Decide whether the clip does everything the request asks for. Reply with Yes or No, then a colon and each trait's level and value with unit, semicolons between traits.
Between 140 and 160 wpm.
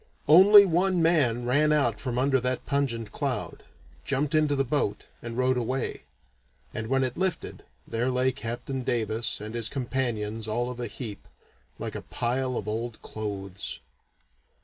Yes: average, 155 wpm